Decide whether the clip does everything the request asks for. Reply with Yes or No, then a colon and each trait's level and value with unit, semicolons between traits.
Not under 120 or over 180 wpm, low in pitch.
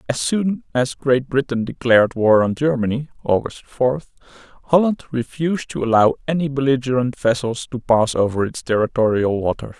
Yes: average, 145 wpm; low, 125 Hz